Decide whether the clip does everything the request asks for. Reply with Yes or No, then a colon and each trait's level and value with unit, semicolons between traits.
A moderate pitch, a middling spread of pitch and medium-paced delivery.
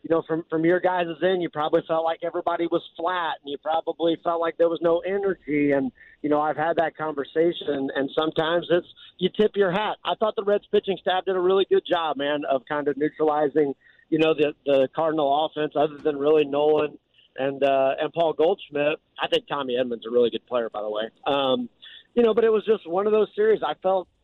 No: medium, 160 Hz; average, 3.3 semitones; fast, 230 wpm